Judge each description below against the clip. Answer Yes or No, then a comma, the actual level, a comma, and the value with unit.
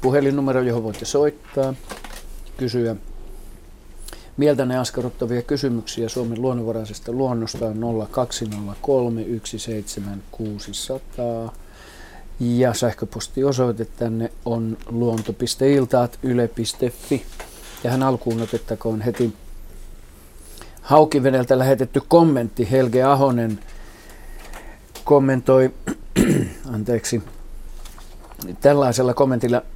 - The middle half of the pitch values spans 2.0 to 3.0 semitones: Yes, average, 2.7 semitones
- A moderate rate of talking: No, slow, 65 wpm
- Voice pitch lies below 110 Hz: No, low, 120 Hz